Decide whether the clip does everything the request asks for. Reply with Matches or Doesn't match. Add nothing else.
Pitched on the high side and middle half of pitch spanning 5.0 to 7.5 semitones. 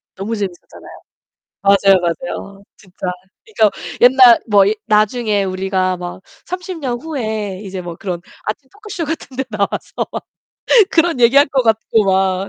Matches